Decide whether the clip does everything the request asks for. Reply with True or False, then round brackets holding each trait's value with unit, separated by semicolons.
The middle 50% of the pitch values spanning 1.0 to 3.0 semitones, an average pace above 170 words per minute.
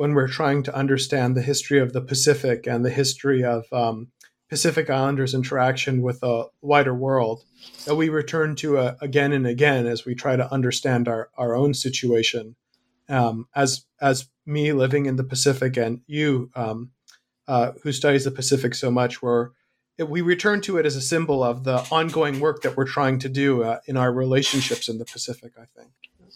True (2.4 semitones; 190 wpm)